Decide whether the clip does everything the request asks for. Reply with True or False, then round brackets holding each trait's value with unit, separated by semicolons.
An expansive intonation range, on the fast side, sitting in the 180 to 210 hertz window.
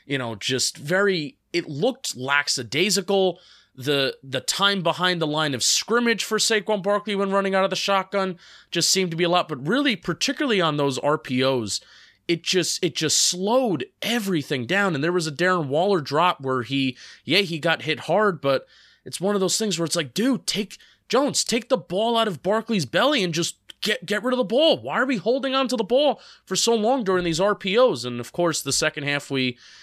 True (5.7 semitones; 210 wpm; 185 Hz)